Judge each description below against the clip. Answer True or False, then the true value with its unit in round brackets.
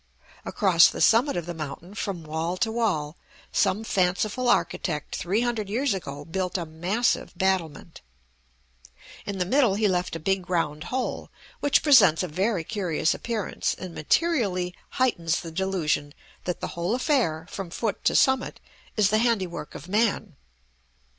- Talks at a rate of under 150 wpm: False (155 wpm)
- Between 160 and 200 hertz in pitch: True (190 Hz)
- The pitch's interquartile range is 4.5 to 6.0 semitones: True (4.9 semitones)